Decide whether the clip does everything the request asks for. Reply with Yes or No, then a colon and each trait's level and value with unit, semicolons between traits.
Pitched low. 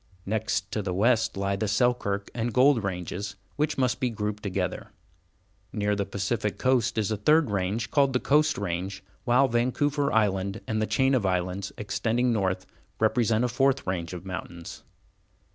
Yes: low, 105 Hz